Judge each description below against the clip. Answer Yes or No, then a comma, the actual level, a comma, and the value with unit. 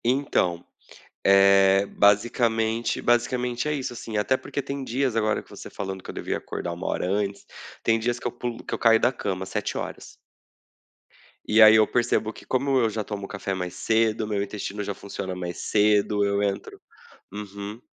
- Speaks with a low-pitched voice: Yes, low, 105 Hz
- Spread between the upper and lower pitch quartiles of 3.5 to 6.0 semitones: No, average, 3.1 semitones